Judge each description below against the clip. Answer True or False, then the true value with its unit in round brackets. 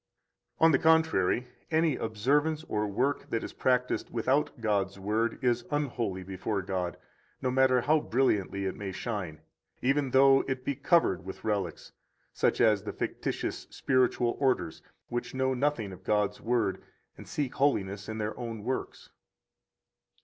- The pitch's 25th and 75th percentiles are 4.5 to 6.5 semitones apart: True (5.1 semitones)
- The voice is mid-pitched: False (120 Hz)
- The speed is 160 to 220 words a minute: False (150 wpm)